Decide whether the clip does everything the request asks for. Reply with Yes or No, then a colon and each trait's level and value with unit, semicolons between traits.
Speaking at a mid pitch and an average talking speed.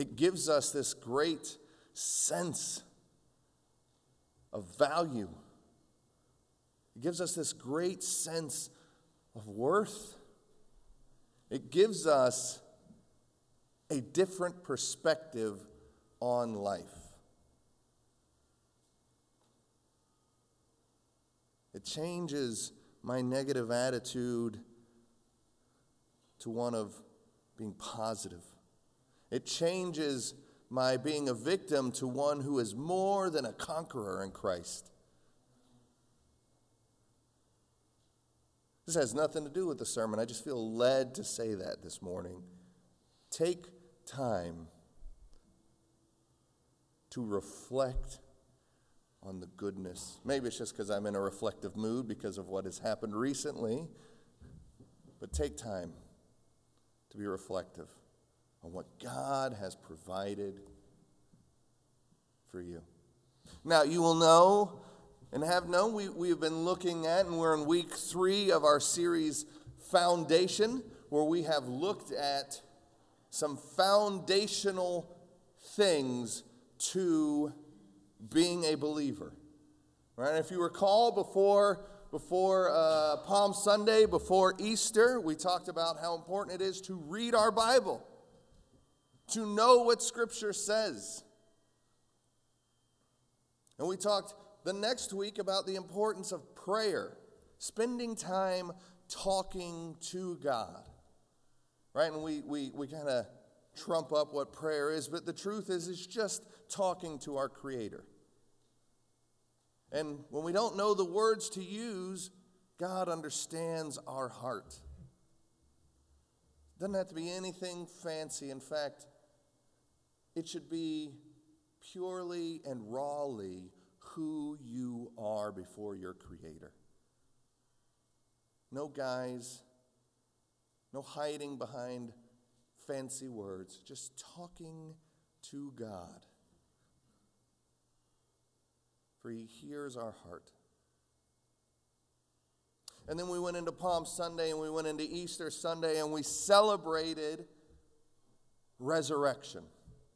No: medium, 150 Hz; slow, 105 wpm